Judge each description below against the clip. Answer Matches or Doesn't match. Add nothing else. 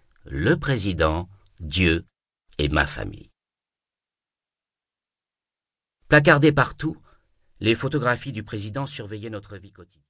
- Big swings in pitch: Matches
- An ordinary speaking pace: Doesn't match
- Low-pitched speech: Matches